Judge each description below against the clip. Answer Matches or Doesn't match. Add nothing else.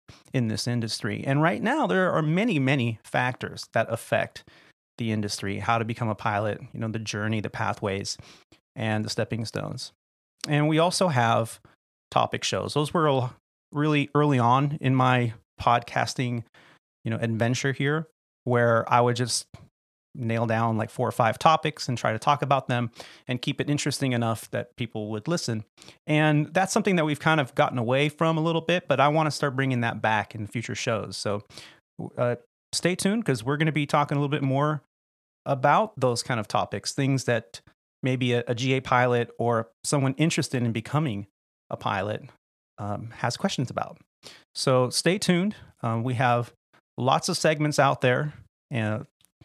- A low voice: Matches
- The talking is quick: Doesn't match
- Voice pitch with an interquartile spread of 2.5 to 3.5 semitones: Doesn't match